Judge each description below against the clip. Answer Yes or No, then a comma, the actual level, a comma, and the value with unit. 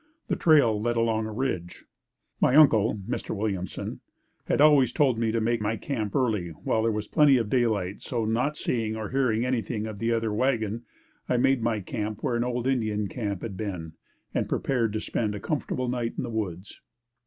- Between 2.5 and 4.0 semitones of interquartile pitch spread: Yes, average, 2.9 semitones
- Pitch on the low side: Yes, low, 115 Hz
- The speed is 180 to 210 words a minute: Yes, average, 195 wpm